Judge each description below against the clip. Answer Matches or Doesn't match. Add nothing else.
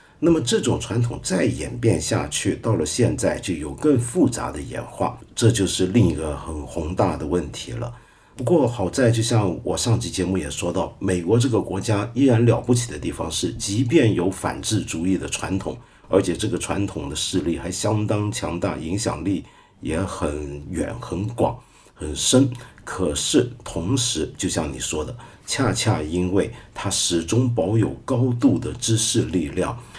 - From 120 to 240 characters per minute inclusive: Doesn't match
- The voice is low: Matches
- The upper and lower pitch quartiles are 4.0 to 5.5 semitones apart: Matches